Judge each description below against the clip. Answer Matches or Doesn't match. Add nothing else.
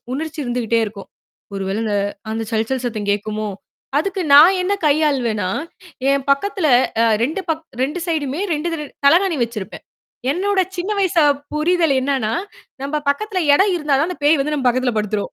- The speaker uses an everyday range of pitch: Doesn't match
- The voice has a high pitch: Matches